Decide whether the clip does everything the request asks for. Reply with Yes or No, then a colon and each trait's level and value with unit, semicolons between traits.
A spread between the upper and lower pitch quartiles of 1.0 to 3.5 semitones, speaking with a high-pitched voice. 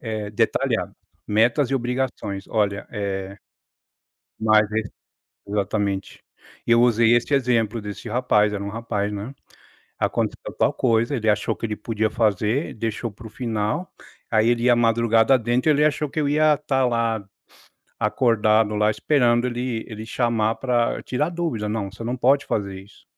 No: average, 2.8 semitones; low, 115 Hz